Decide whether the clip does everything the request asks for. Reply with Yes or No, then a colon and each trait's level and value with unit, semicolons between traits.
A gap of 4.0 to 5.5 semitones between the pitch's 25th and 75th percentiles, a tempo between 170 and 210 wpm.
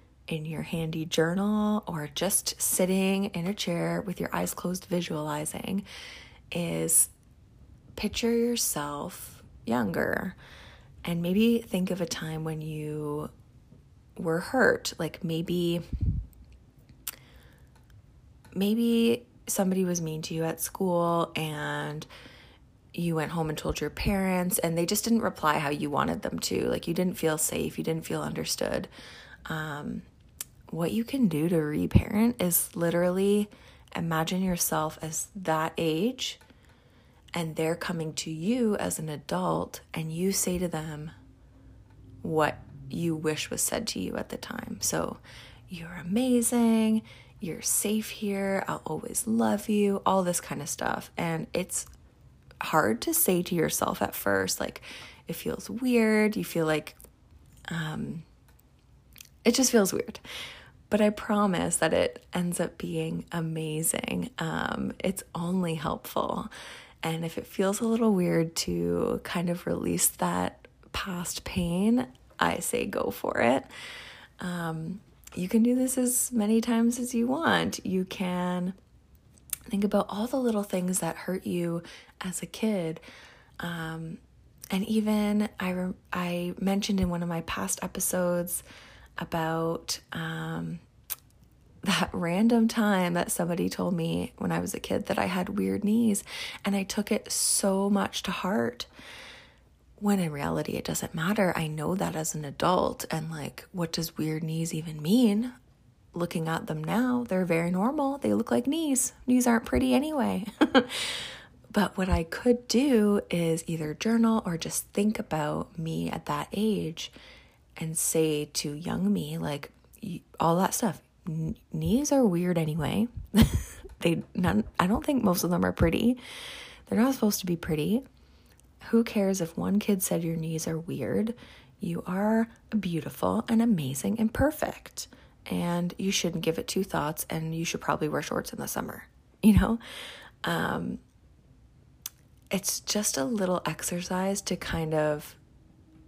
No: average, 4.8 semitones; average, 150 wpm